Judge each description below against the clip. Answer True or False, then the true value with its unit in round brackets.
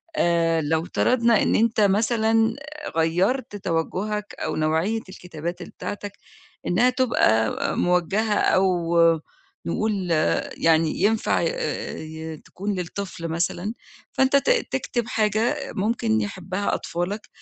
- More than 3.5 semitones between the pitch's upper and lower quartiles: True (5.0 semitones)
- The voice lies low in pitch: False (195 Hz)